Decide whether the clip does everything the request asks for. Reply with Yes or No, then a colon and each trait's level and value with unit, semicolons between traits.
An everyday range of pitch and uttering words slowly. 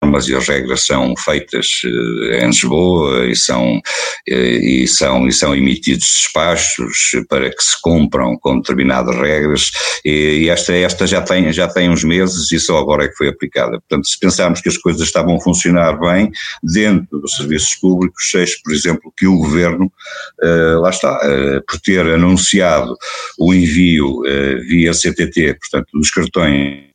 No: average, 4.2 semitones; average, 165 wpm